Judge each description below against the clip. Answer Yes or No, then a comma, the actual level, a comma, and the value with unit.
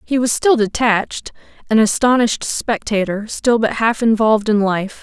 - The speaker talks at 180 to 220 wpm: No, average, 155 wpm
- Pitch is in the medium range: No, high, 220 Hz